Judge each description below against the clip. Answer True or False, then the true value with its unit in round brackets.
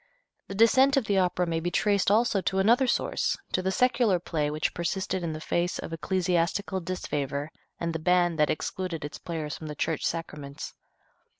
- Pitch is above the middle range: False (175 Hz)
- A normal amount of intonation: True (3.2 semitones)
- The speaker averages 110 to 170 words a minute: False (185 wpm)